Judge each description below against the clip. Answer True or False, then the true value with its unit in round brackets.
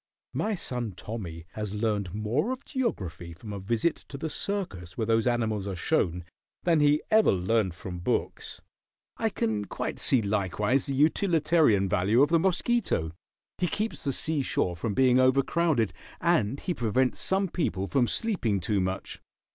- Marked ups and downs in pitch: True (8.3 semitones)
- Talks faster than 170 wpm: False (165 wpm)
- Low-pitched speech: True (115 Hz)